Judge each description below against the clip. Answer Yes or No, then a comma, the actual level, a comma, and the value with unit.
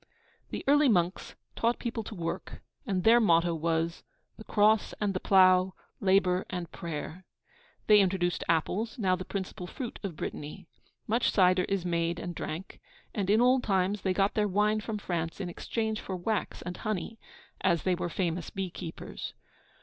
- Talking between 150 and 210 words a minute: Yes, average, 175 wpm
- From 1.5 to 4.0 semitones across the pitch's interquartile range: Yes, average, 3.3 semitones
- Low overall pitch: No, medium, 185 Hz